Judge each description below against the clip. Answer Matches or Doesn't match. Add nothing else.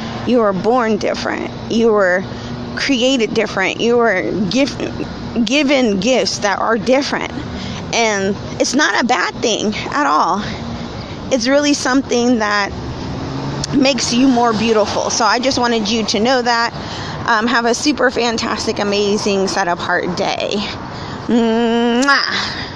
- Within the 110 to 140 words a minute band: Matches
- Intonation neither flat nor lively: Matches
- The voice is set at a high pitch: Matches